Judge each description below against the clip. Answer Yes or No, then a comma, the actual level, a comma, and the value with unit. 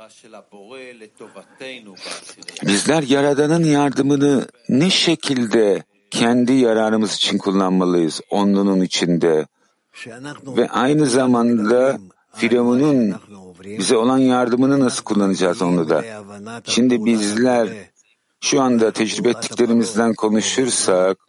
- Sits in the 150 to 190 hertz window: No, low, 115 Hz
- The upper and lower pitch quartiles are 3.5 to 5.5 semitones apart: Yes, average, 4.4 semitones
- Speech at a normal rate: No, slow, 80 wpm